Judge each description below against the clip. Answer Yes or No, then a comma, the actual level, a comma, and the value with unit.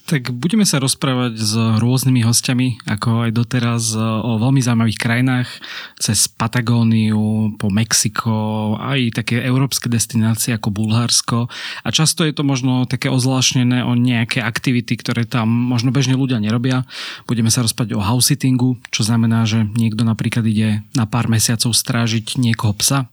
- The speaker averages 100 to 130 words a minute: No, average, 150 wpm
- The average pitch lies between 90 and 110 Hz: No, low, 120 Hz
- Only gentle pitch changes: Yes, narrow, 2.1 semitones